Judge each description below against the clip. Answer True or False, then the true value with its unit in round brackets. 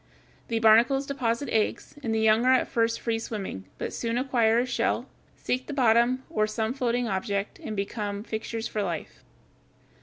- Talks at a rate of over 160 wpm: True (175 wpm)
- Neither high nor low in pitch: False (230 Hz)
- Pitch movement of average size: False (2.3 semitones)